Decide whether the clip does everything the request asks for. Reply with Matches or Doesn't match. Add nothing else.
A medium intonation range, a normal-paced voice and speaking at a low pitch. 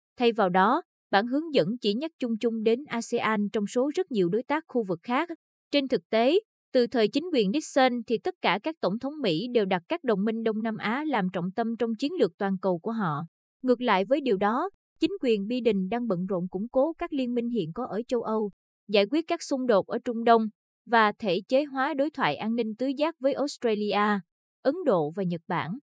Doesn't match